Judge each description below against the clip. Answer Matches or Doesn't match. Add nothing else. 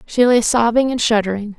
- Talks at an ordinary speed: Matches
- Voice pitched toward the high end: Matches